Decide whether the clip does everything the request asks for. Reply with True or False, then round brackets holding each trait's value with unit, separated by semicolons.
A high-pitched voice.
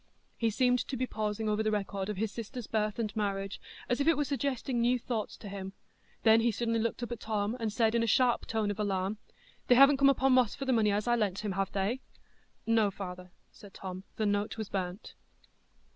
True (220 Hz)